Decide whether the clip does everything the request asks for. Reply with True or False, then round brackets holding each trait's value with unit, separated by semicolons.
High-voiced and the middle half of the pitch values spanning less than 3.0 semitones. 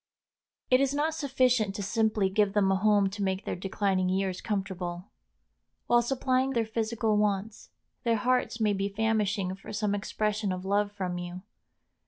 True (205 Hz; 2.6 semitones)